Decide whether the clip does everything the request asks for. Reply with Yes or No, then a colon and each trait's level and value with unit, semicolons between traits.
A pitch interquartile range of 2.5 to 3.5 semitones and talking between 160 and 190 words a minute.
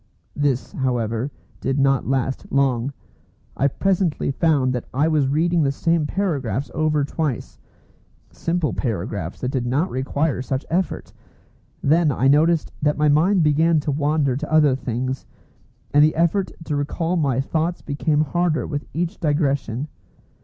No: average, 3.2 semitones; average, 145 wpm